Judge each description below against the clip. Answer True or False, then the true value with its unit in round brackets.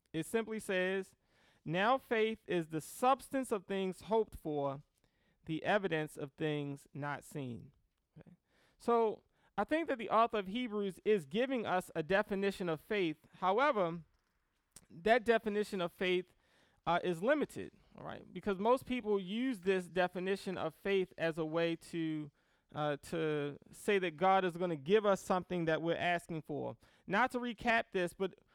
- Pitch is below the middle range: False (185 Hz)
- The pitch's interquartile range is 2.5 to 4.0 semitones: False (4.7 semitones)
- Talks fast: False (160 wpm)